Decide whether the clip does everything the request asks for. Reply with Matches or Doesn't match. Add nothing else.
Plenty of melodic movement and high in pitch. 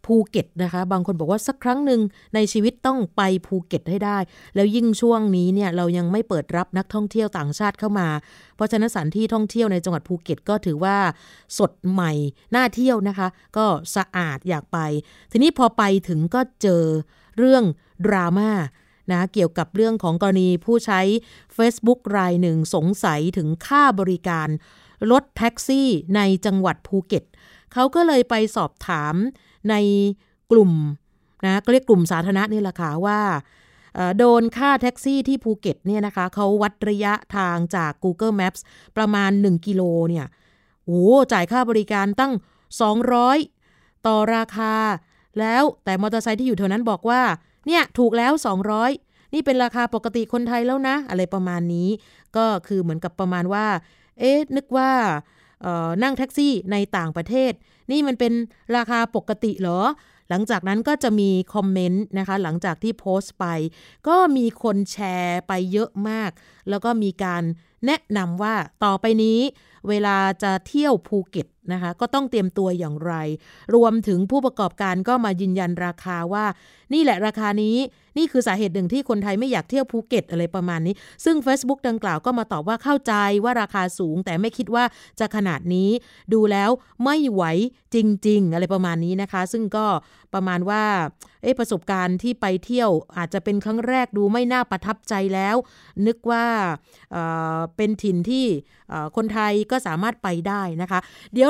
Doesn't match